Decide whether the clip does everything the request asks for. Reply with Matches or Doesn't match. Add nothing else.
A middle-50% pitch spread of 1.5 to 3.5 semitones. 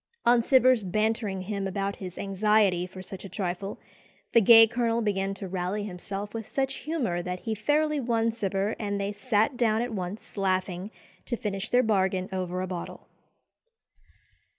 Matches